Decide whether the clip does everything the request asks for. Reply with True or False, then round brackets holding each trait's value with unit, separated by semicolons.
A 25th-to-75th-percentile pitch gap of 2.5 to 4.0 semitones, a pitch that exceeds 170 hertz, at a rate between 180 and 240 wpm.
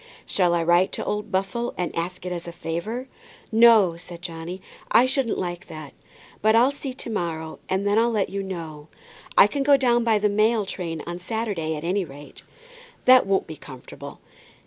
False (4.9 semitones; 190 Hz; 190 wpm)